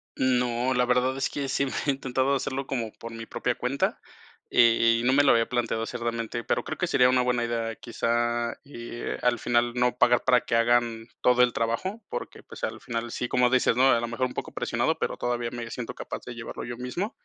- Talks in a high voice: No, low, 120 Hz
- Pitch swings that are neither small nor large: No, narrow, 1.5 semitones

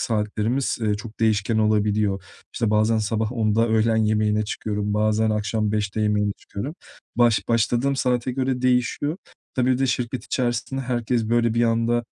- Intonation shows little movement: Yes, narrow, 2.2 semitones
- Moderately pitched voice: No, low, 110 Hz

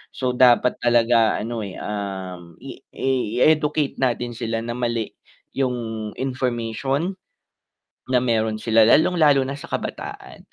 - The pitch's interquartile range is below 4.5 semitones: Yes, average, 2.9 semitones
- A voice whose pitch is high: No, low, 120 Hz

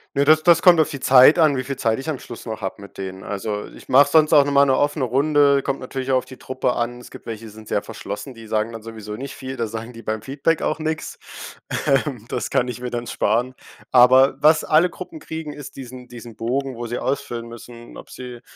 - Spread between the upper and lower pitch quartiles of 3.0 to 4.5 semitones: Yes, average, 3.4 semitones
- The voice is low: Yes, low, 130 Hz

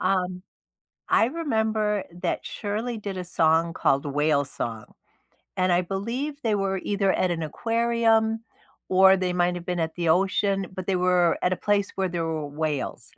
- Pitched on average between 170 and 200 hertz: Yes, medium, 185 Hz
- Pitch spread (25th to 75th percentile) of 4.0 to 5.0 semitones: No, average, 3.6 semitones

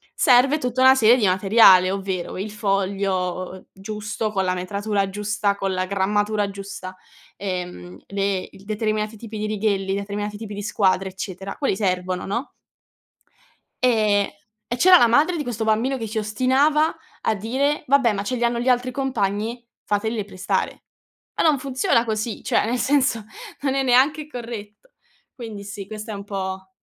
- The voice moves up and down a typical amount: Yes, average, 3.6 semitones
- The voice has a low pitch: No, high, 210 Hz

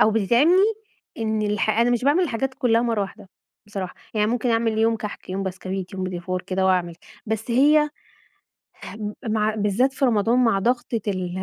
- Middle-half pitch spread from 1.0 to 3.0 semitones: No, average, 3.7 semitones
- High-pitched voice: Yes, high, 220 Hz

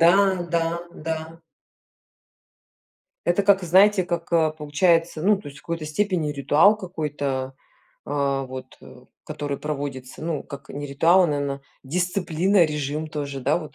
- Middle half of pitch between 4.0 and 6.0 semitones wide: No, average, 3.4 semitones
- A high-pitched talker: No, medium, 155 Hz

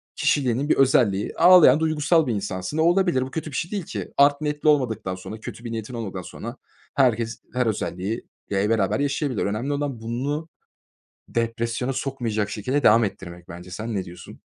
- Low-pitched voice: Yes, low, 120 Hz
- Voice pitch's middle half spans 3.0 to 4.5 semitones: No, average, 5.2 semitones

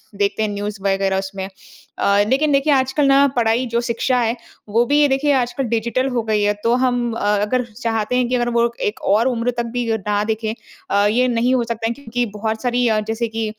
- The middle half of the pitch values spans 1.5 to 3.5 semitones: Yes, narrow, 2.6 semitones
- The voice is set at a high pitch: Yes, high, 235 Hz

